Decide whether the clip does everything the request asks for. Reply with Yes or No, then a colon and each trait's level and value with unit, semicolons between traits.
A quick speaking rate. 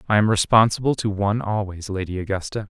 No: average, 175 wpm